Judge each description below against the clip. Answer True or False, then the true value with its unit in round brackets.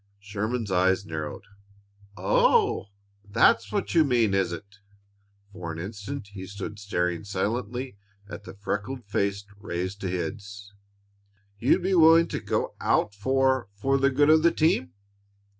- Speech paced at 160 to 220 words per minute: False (140 wpm)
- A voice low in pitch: True (100 Hz)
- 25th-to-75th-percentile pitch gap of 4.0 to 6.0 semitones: True (4.9 semitones)